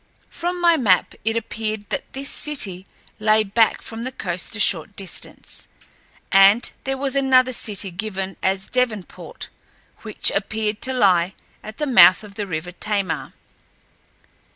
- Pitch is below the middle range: No, high, 215 Hz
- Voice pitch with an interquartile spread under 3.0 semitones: No, average, 4.6 semitones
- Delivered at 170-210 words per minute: No, average, 145 wpm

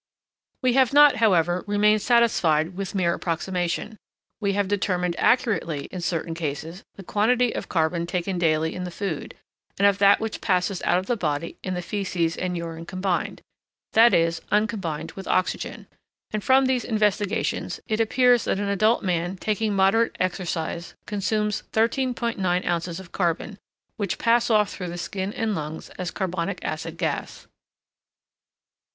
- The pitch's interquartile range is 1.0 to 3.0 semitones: No, average, 3.9 semitones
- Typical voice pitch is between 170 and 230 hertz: Yes, high, 190 Hz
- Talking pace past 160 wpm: No, average, 155 wpm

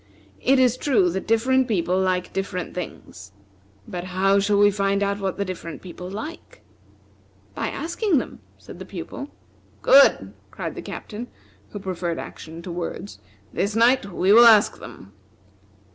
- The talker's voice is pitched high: Yes, high, 200 Hz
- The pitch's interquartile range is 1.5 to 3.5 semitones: No, average, 4.5 semitones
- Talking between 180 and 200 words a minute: No, average, 155 wpm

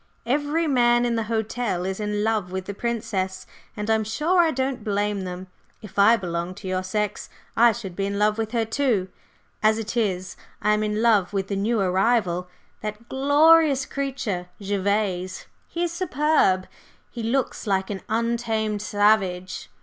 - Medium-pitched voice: No, high, 215 Hz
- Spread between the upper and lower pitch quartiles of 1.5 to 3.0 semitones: No, average, 3.7 semitones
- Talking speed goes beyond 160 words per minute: Yes, average, 170 wpm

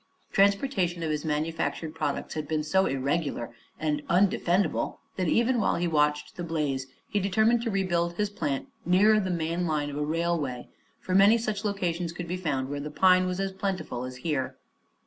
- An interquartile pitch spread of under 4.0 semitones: No, average, 4.3 semitones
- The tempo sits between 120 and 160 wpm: No, average, 185 wpm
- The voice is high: No, medium, 170 Hz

